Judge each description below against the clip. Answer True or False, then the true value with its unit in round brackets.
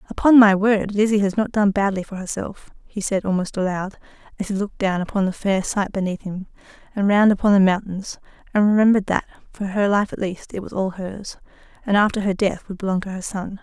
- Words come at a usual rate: False (220 wpm)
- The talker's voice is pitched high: True (200 Hz)